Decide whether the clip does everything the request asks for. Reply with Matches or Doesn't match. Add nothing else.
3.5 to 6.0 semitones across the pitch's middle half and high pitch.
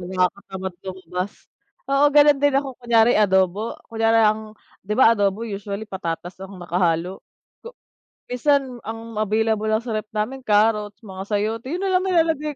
Matches